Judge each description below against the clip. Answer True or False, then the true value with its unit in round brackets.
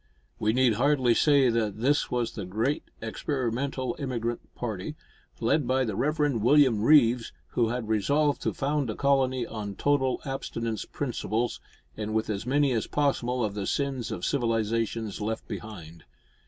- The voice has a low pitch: True (120 Hz)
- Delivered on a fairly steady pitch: False (3.9 semitones)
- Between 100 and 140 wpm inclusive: False (155 wpm)